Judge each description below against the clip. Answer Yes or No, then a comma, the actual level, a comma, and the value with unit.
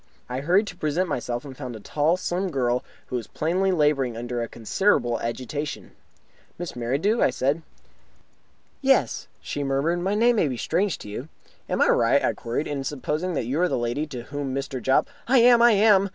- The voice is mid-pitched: Yes, medium, 145 Hz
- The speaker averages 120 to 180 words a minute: No, average, 200 wpm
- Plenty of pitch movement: Yes, wide, 6.5 semitones